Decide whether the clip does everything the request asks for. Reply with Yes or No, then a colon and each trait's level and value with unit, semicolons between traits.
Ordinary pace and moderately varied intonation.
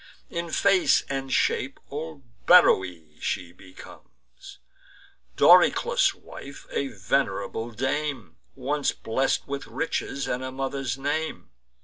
No: slow, 105 wpm; average, 4.7 semitones